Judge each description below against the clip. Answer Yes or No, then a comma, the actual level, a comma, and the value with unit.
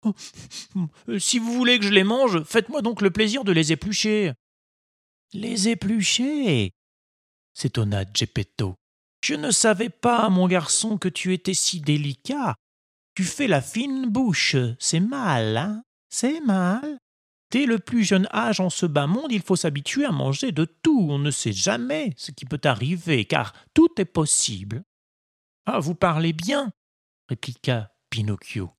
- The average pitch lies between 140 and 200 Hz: Yes, medium, 185 Hz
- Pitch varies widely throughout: Yes, wide, 8.5 semitones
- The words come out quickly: No, average, 160 wpm